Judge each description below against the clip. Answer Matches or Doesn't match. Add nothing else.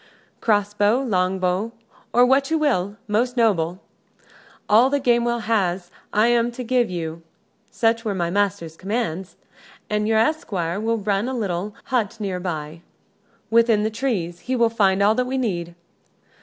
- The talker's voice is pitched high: Matches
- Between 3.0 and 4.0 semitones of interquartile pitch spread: Doesn't match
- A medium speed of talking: Matches